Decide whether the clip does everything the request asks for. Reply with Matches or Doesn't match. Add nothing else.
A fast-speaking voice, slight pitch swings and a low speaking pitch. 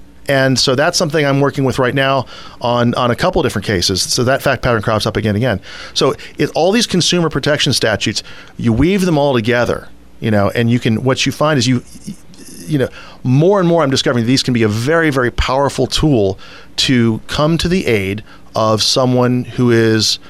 Doesn't match